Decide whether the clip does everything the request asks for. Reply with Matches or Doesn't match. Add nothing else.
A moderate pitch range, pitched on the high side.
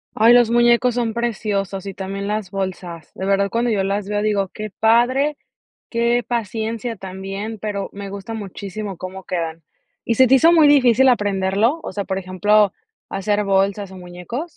Matches